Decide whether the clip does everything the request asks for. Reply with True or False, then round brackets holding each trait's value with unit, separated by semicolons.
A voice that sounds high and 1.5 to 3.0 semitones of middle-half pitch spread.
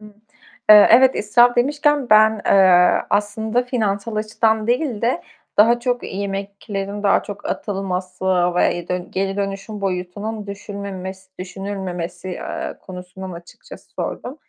True (200 Hz; 2.6 semitones)